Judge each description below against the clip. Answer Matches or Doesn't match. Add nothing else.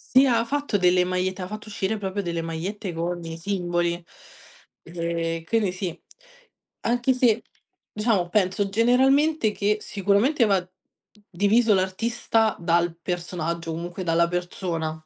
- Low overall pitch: Doesn't match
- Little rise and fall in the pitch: Doesn't match